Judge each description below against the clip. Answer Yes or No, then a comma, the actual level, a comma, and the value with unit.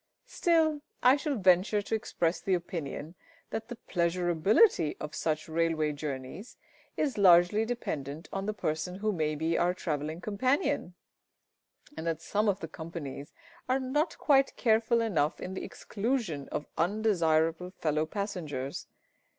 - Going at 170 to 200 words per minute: No, average, 140 wpm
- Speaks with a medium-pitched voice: Yes, medium, 180 Hz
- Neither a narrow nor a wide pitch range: No, wide, 5.7 semitones